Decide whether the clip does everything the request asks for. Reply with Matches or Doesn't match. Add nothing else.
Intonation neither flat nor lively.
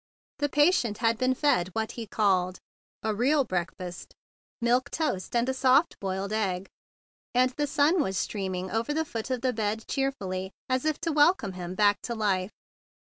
Doesn't match